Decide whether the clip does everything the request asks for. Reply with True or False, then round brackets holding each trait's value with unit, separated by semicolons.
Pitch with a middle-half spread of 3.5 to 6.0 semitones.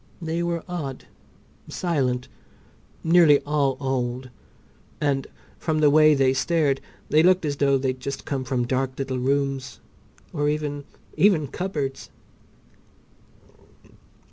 False (2.8 semitones)